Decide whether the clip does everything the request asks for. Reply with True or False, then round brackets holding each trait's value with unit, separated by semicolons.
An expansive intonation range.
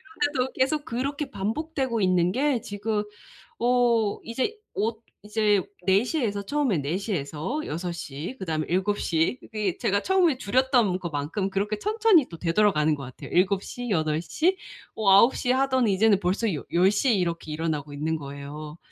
True (6.9 semitones)